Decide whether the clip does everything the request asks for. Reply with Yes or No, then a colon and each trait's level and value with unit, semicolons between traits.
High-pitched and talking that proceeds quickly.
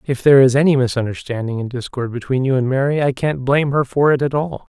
No: low, 135 Hz; fast, 240 wpm